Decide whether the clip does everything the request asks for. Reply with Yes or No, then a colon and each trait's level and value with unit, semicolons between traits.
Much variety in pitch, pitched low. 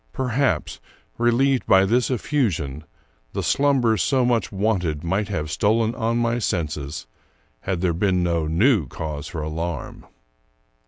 Yes: wide, 6.7 semitones; very low, 95 Hz